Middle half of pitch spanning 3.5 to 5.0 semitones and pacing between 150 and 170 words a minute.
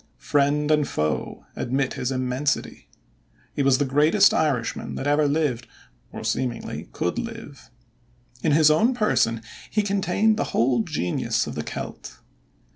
No: average, 4.0 semitones; average, 140 wpm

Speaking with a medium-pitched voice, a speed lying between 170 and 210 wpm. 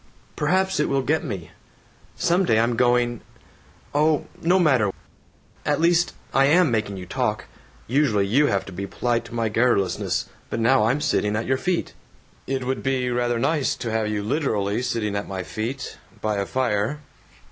No: low, 120 Hz; average, 175 wpm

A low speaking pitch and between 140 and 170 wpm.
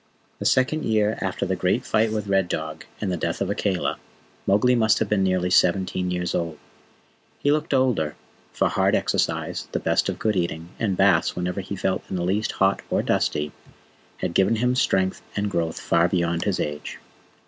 No: very low, 95 Hz; average, 190 wpm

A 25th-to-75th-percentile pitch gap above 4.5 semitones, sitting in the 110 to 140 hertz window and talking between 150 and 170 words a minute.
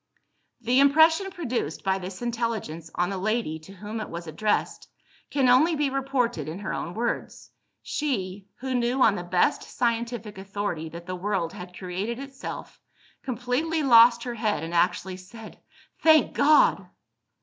No: wide, 5.6 semitones; high, 220 Hz; average, 155 wpm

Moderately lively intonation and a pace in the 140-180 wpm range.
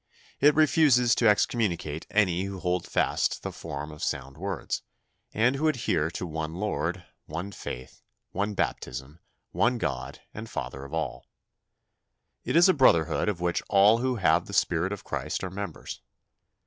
No: wide, 5.9 semitones; average, 160 wpm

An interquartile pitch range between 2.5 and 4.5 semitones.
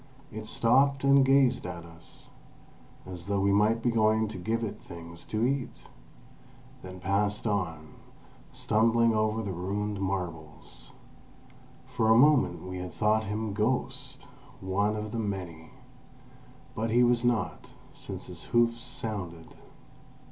Yes: average, 3.9 semitones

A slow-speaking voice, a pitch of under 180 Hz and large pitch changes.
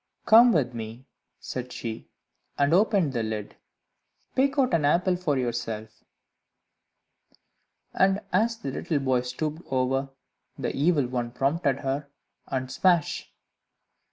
Yes: slow, 125 wpm; medium, 140 Hz; wide, 6.0 semitones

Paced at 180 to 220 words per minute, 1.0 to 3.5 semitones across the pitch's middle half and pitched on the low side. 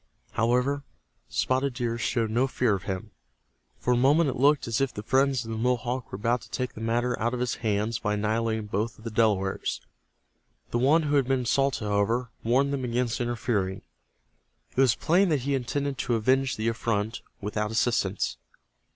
Yes: average, 185 wpm; average, 3.0 semitones; low, 120 Hz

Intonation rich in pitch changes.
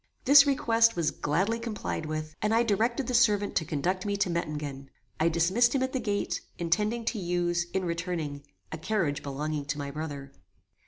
Yes: wide, 6.3 semitones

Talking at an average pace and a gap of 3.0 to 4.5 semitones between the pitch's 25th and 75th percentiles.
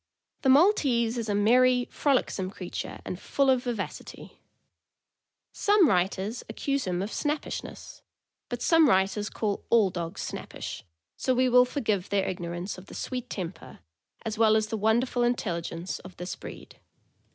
No: average, 150 wpm; average, 4.9 semitones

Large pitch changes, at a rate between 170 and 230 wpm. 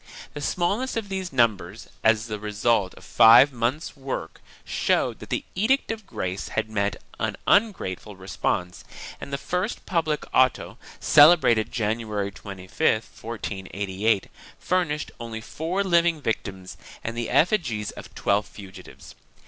No: wide, 8.4 semitones; average, 140 wpm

